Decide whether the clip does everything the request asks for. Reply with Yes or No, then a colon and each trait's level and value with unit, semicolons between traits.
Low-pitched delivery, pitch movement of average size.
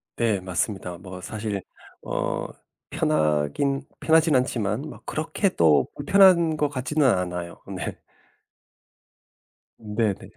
No: low, 110 Hz; wide, 8.4 semitones